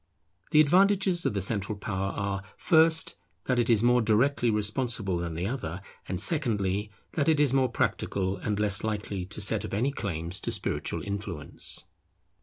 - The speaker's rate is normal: Yes, average, 170 wpm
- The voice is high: No, low, 105 Hz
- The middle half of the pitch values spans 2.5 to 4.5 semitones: No, average, 5.3 semitones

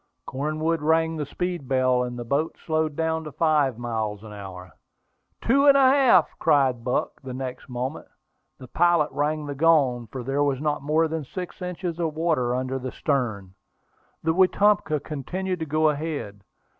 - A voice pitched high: No, medium, 150 Hz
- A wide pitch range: No, average, 4.2 semitones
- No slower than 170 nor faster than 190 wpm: Yes, average, 175 wpm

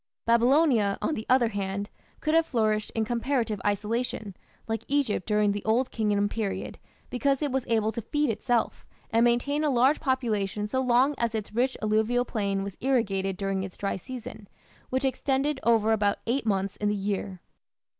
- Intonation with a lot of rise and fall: No, average, 3.9 semitones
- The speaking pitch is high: Yes, high, 225 Hz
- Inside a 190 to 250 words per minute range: No, average, 175 wpm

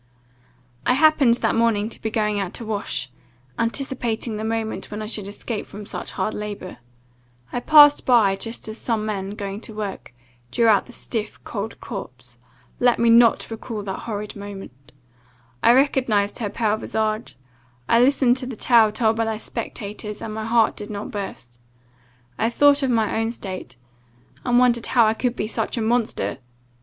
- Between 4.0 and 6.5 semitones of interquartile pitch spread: No, narrow, 2.4 semitones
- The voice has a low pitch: No, high, 220 Hz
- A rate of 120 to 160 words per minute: No, average, 175 wpm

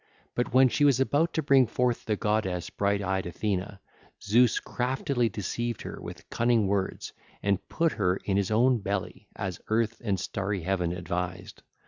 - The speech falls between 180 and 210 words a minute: No, average, 165 wpm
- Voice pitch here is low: Yes, low, 105 Hz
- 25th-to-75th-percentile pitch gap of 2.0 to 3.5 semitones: No, average, 4.2 semitones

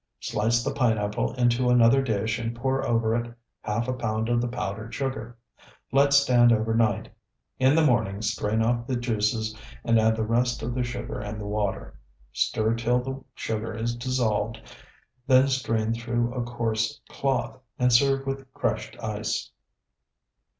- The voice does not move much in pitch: Yes, narrow, 2.2 semitones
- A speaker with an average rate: Yes, average, 155 wpm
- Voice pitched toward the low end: Yes, low, 120 Hz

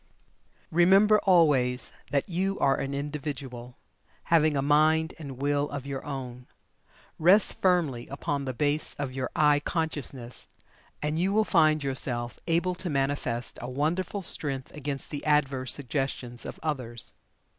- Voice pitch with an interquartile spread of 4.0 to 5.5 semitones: No, average, 3.3 semitones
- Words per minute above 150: No, average, 140 wpm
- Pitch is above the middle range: No, medium, 145 Hz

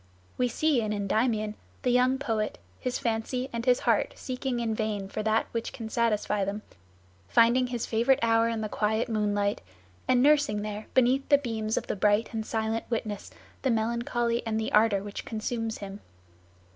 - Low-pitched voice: No, high, 225 Hz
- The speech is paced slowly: No, average, 175 wpm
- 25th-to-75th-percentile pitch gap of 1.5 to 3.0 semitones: Yes, narrow, 2.4 semitones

